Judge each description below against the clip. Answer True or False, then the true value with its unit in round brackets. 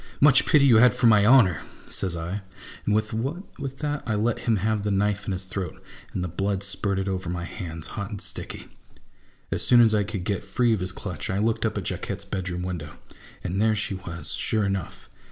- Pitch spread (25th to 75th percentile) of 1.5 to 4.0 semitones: True (3.1 semitones)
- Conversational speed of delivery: False (220 wpm)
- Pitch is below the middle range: True (100 Hz)